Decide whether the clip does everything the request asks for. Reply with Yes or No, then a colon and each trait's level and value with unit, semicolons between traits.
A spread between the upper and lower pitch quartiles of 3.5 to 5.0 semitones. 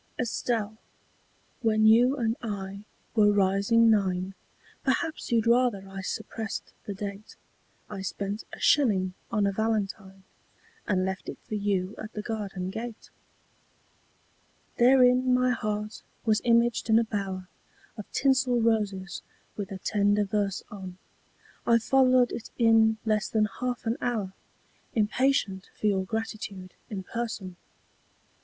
No: average, 3.0 semitones